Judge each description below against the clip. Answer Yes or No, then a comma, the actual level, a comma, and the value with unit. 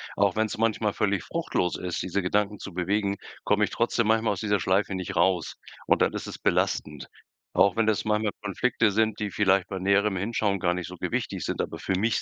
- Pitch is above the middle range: No, low, 100 Hz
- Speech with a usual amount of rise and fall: No, narrow, 2.3 semitones